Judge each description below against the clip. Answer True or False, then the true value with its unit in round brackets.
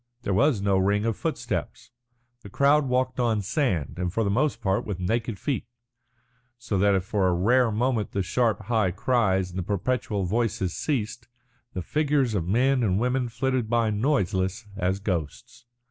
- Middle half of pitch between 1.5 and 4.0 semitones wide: False (4.6 semitones)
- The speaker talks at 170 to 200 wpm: True (175 wpm)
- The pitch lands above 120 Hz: False (110 Hz)